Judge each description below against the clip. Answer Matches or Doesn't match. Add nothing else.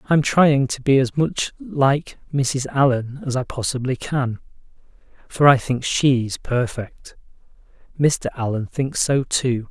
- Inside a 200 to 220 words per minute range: Doesn't match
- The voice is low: Matches